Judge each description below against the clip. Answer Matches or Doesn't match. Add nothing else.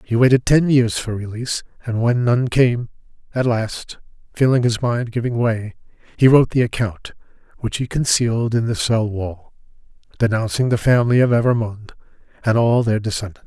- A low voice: Matches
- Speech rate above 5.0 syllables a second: Matches